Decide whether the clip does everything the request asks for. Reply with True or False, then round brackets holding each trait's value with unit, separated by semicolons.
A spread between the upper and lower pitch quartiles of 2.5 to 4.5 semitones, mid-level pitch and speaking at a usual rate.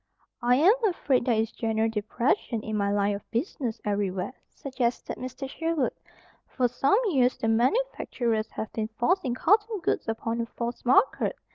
False (3.6 semitones; 240 Hz; 155 wpm)